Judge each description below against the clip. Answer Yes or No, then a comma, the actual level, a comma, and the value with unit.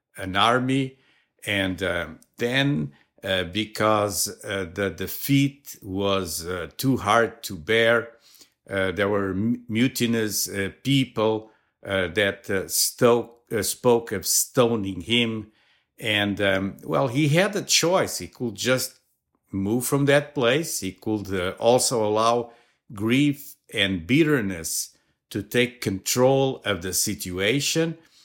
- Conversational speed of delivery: No, slow, 125 wpm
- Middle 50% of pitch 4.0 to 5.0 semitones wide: Yes, average, 4.6 semitones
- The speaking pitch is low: Yes, low, 110 Hz